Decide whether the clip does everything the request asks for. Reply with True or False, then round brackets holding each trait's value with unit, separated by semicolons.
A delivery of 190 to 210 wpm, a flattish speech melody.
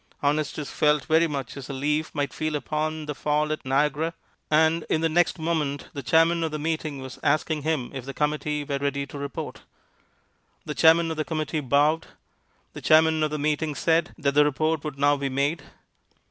True (195 wpm; 1.9 semitones)